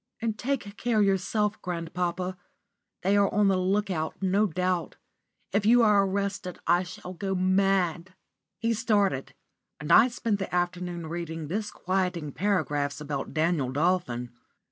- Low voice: No, medium, 185 Hz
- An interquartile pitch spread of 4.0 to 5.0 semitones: No, average, 3.0 semitones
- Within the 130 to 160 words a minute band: Yes, average, 140 wpm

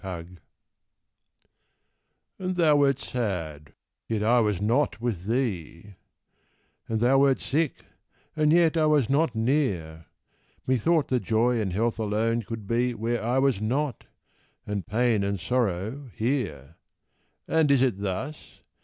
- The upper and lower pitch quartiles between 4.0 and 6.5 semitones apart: Yes, average, 5.2 semitones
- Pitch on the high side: No, low, 115 Hz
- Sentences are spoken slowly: Yes, slow, 130 wpm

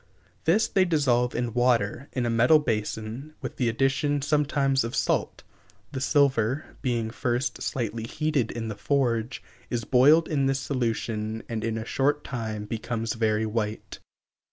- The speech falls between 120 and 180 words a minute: Yes, average, 155 wpm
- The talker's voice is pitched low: Yes, low, 120 Hz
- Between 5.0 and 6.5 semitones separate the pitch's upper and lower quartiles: No, average, 3.7 semitones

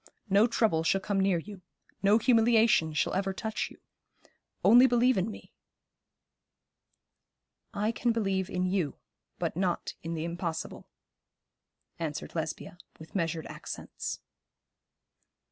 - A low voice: No, high, 195 Hz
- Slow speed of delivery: Yes, slow, 120 wpm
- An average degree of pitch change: Yes, average, 4.7 semitones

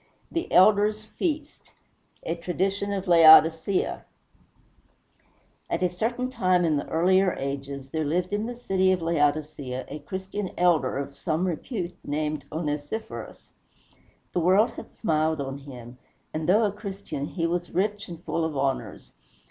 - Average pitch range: Yes, average, 4.5 semitones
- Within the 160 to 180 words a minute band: No, average, 145 wpm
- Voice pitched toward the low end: No, medium, 175 Hz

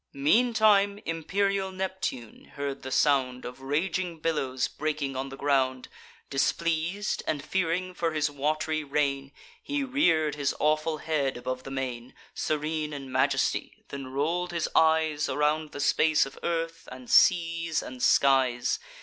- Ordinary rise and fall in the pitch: Yes, average, 3.5 semitones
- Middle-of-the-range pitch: Yes, medium, 150 Hz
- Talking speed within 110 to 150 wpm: Yes, average, 140 wpm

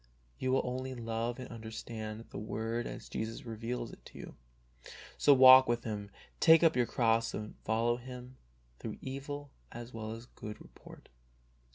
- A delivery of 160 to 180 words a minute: Yes, average, 165 wpm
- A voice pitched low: Yes, low, 120 Hz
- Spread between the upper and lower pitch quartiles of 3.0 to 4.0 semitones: No, narrow, 2.4 semitones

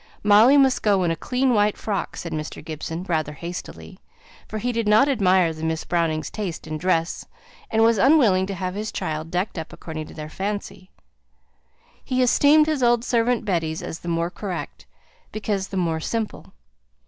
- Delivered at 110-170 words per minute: No, average, 180 wpm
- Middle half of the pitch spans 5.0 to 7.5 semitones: Yes, wide, 5.5 semitones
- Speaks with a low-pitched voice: No, high, 190 Hz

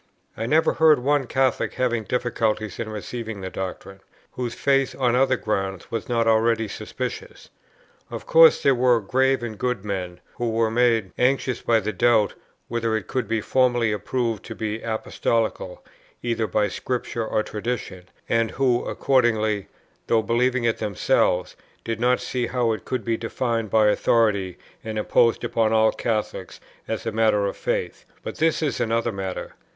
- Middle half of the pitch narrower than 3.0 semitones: Yes, narrow, 2.4 semitones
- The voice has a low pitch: Yes, low, 115 Hz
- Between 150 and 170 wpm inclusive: Yes, average, 165 wpm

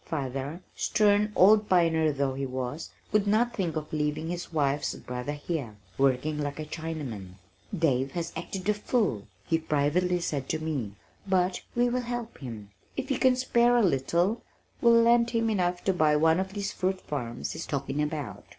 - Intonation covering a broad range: Yes, wide, 6.4 semitones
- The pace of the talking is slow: No, average, 180 wpm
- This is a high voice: No, medium, 160 Hz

